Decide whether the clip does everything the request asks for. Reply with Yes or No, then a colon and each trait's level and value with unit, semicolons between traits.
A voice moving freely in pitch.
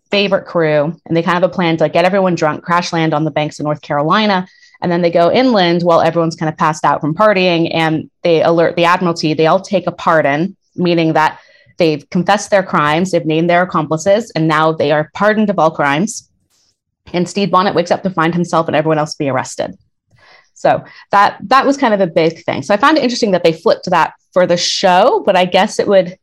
No: average, 3.2 semitones